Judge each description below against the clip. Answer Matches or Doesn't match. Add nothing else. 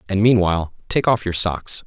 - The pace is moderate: Matches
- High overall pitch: Doesn't match